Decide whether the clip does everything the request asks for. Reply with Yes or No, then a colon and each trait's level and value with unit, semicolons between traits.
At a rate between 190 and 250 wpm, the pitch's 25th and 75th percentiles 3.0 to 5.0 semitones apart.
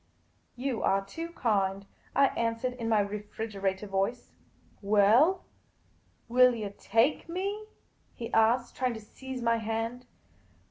No: average, 140 wpm; average, 3.4 semitones